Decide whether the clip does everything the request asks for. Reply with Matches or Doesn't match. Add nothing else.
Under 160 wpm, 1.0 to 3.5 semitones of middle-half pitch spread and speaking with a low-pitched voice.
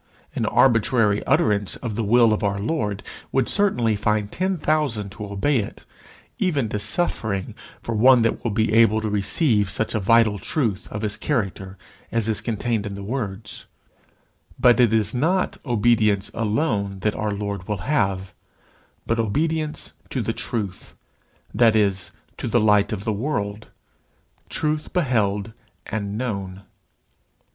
Matches